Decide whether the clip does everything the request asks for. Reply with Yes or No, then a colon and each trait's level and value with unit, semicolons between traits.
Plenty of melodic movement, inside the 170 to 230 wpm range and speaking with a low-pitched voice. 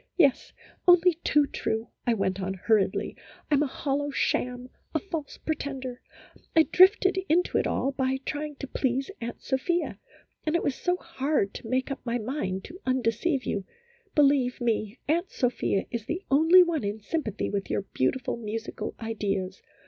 No: wide, 5.7 semitones; average, 175 wpm; very high, 265 Hz